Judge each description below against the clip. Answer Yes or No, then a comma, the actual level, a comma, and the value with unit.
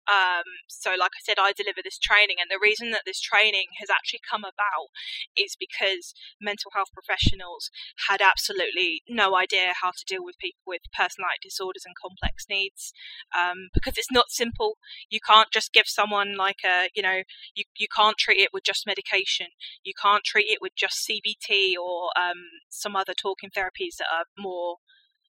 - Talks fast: No, average, 185 wpm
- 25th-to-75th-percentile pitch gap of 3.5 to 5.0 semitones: Yes, average, 4.1 semitones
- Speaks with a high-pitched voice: Yes, high, 205 Hz